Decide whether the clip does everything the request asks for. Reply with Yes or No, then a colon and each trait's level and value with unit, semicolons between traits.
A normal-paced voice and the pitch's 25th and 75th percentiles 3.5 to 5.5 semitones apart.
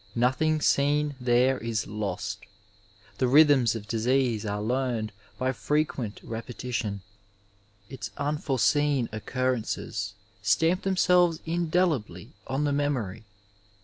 No: slow, 100 wpm; average, 5.0 semitones